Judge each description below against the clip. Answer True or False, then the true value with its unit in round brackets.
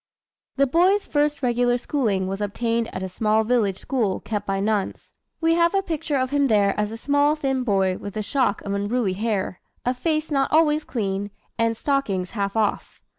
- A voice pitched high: True (230 Hz)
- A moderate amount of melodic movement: False (5.9 semitones)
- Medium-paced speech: True (190 wpm)